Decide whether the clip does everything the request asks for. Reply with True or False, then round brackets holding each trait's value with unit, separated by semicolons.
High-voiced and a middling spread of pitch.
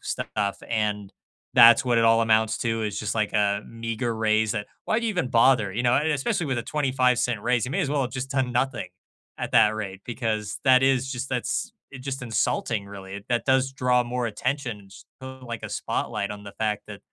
False (115 Hz; 3.2 semitones)